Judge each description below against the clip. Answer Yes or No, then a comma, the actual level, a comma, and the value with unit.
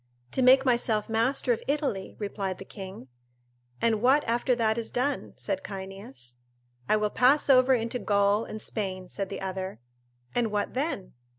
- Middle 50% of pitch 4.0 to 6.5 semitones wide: Yes, average, 4.4 semitones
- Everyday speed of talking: Yes, average, 165 wpm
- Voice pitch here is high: Yes, high, 220 Hz